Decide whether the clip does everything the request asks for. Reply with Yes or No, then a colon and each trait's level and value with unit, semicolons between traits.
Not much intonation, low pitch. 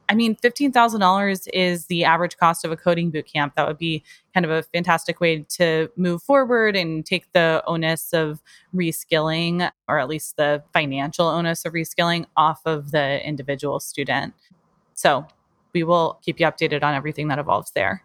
No: narrow, 2.1 semitones; medium, 165 Hz